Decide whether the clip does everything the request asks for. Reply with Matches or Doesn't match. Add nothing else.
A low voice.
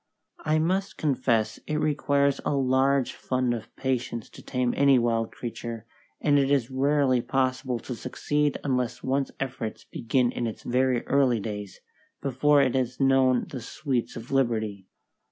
Matches